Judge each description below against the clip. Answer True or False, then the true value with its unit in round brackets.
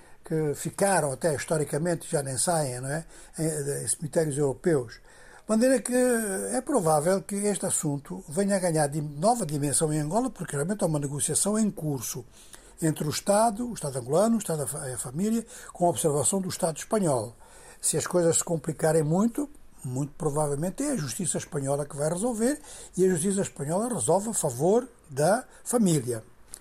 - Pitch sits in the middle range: True (170 Hz)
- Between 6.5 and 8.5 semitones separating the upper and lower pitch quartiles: False (5.2 semitones)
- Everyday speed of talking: True (165 wpm)